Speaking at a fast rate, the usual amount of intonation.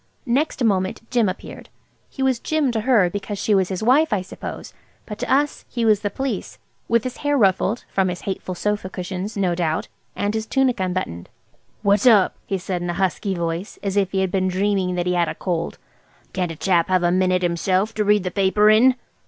Yes: fast, 210 wpm; average, 3.2 semitones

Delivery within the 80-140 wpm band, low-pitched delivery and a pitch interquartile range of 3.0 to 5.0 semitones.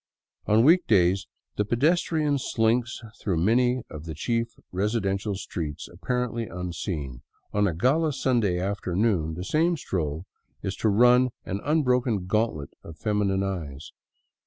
No: slow, 135 wpm; low, 105 Hz; wide, 5.5 semitones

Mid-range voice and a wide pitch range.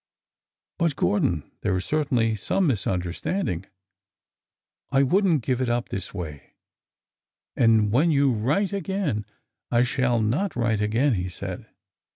No: low, 120 Hz; wide, 5.8 semitones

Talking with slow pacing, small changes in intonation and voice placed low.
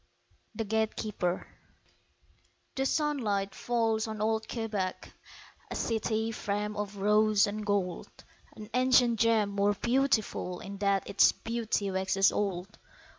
No: slow, 120 wpm; narrow, 2.1 semitones; high, 210 Hz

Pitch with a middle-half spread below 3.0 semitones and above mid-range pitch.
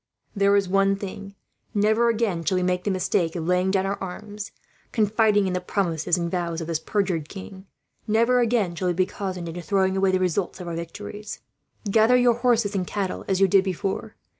Yes: narrow, 2.4 semitones; high, 195 Hz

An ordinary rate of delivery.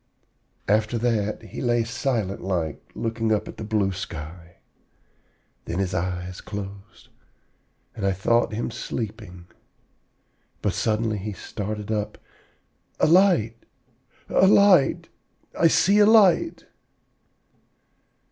No: slow, 110 wpm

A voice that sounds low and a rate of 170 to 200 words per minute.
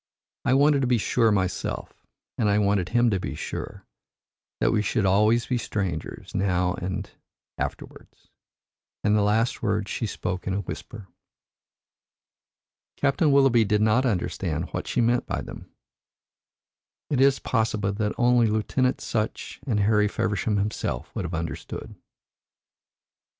No: low, 105 Hz; average, 145 wpm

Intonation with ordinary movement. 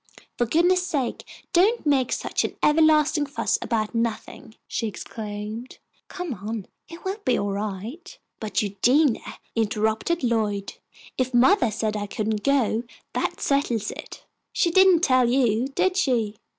No: wide, 6.1 semitones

